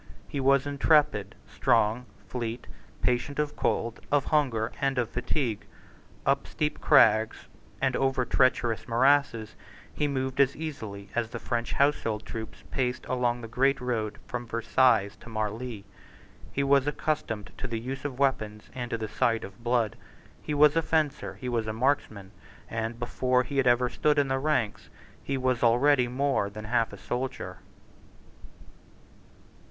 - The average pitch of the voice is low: Yes, low, 125 Hz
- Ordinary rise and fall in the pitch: Yes, average, 3.4 semitones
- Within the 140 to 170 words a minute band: Yes, average, 155 wpm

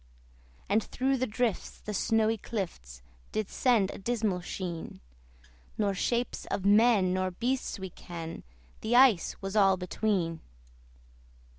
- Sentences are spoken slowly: Yes, slow, 130 wpm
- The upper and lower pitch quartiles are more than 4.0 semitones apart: No, average, 3.7 semitones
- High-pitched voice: Yes, high, 205 Hz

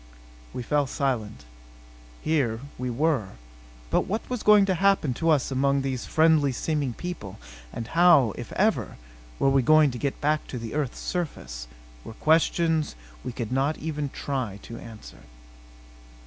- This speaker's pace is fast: No, average, 155 wpm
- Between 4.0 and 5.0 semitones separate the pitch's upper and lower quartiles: Yes, average, 4.5 semitones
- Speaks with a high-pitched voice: No, medium, 140 Hz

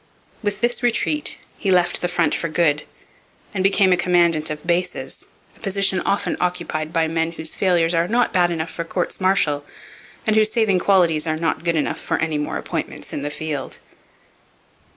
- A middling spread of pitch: Yes, average, 3.1 semitones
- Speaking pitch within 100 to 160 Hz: No, medium, 175 Hz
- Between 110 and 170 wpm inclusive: No, average, 180 wpm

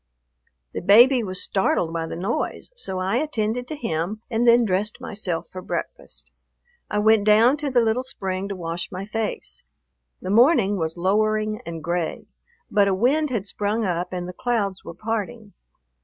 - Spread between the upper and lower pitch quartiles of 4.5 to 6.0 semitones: No, average, 4.0 semitones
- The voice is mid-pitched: No, high, 210 Hz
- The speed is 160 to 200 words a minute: Yes, average, 170 wpm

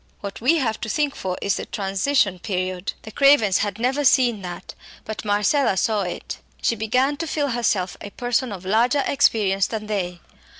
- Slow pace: No, average, 180 wpm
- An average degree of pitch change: Yes, average, 4.9 semitones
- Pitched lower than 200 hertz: No, high, 215 Hz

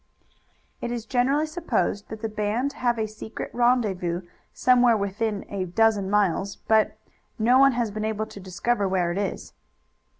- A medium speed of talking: Yes, average, 160 wpm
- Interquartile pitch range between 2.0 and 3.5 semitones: Yes, average, 3.2 semitones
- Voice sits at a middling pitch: No, high, 220 Hz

